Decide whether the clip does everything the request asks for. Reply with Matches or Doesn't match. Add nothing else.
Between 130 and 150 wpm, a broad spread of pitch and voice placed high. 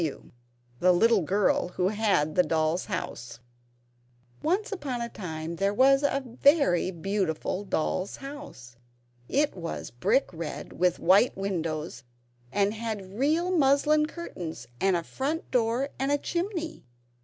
Matches